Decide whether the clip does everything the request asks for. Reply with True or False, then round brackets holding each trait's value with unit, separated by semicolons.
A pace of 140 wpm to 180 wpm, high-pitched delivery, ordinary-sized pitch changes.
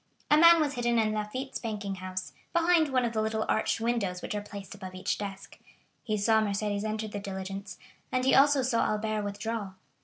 False (195 wpm; 215 Hz; 3.1 semitones)